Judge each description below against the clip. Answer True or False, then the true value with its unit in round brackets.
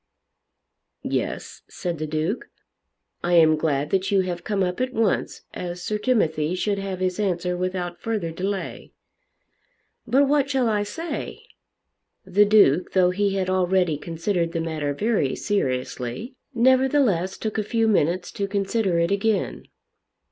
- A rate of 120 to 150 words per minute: True (145 wpm)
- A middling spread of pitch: True (3.9 semitones)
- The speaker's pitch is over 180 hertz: True (190 Hz)